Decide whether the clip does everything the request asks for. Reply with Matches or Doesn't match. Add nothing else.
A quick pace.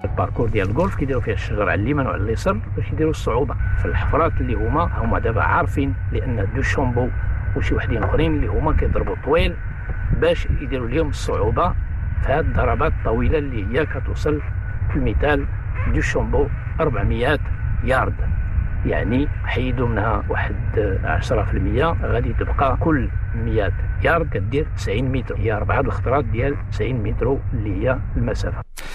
Matches